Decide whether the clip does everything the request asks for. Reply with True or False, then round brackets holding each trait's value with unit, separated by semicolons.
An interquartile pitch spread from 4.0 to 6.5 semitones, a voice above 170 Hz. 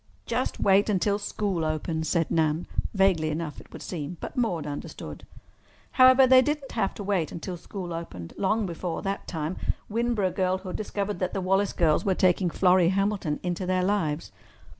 False (3.5 semitones; 185 Hz)